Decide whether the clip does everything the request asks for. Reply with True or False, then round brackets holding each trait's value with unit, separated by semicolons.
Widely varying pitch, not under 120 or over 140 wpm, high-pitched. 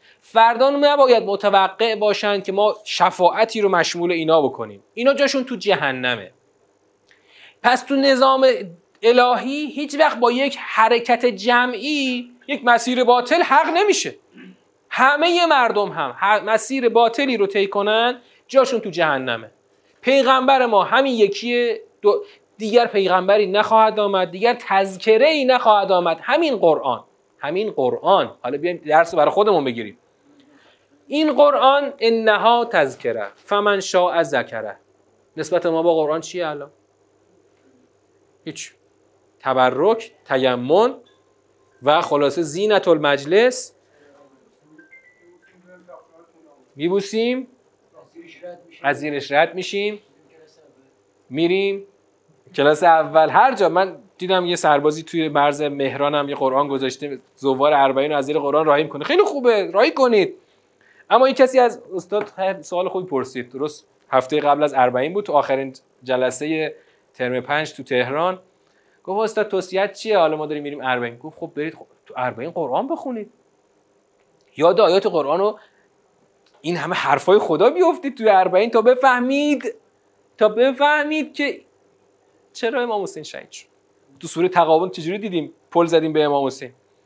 True (8.6 semitones; 125 wpm; 205 Hz)